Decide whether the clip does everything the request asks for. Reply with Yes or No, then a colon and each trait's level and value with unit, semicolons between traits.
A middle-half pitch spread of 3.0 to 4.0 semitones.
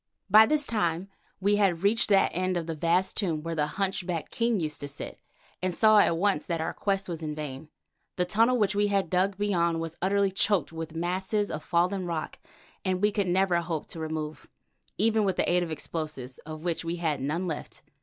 Yes: average, 3.6 semitones